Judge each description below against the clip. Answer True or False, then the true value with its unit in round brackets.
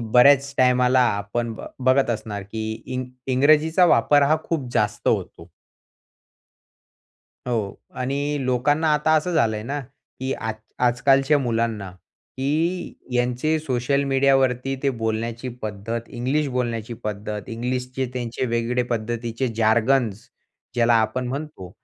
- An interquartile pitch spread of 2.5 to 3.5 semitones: True (3.2 semitones)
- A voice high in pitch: False (125 Hz)